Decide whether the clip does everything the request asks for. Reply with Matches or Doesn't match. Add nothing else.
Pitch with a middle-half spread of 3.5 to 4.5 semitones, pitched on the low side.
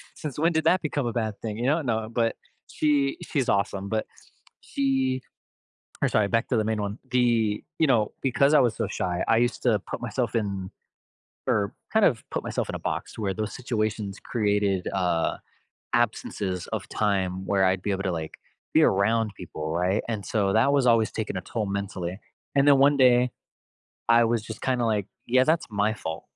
Matches